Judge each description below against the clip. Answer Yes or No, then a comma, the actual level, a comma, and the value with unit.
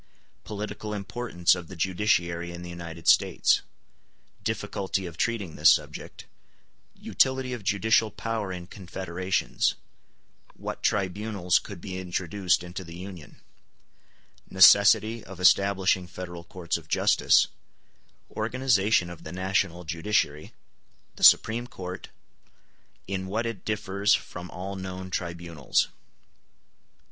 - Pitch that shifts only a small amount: No, average, 3.1 semitones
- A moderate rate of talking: No, slow, 100 wpm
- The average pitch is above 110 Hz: No, very low, 95 Hz